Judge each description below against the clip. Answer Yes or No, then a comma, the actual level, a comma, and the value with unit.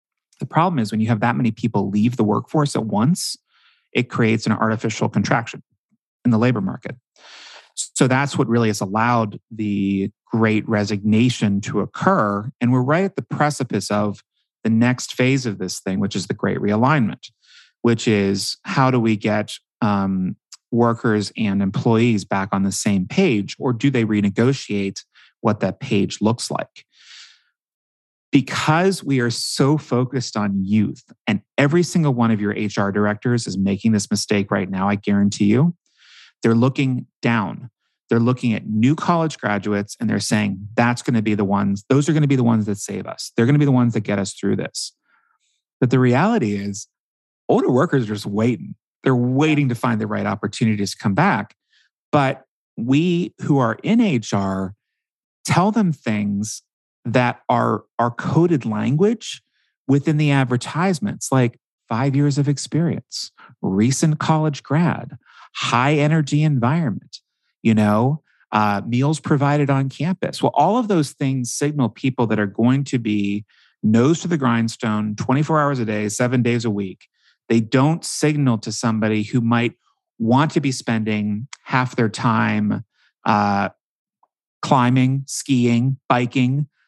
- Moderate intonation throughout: Yes, average, 4.6 semitones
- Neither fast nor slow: Yes, average, 160 wpm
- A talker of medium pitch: No, low, 120 Hz